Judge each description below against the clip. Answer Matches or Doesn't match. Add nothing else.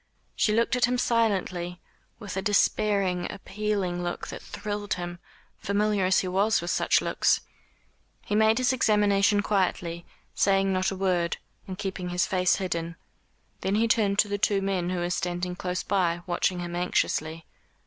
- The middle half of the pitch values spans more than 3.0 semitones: Doesn't match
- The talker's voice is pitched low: Doesn't match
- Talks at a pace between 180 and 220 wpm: Doesn't match